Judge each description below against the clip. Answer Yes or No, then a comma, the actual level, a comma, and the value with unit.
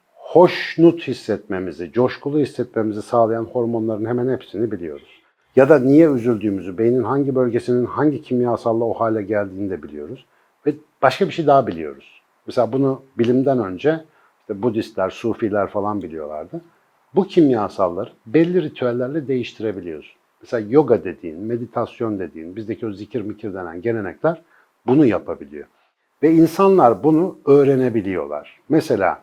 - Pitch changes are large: No, average, 4.7 semitones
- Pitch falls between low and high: No, low, 120 Hz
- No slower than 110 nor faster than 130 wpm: Yes, average, 125 wpm